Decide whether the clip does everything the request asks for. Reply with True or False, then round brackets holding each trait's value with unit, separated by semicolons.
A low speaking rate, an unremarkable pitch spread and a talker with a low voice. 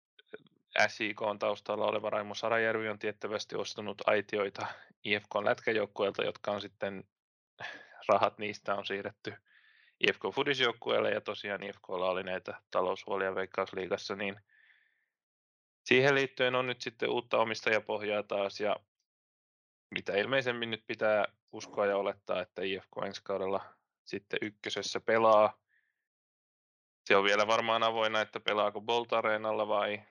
False (125 wpm; 3.7 semitones; 110 Hz)